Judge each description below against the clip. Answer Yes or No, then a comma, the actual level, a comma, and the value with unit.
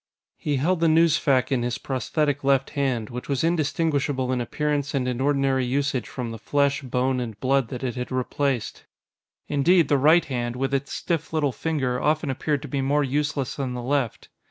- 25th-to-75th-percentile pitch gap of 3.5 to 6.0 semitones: No, narrow, 2.5 semitones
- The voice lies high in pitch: No, low, 135 Hz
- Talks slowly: No, average, 190 wpm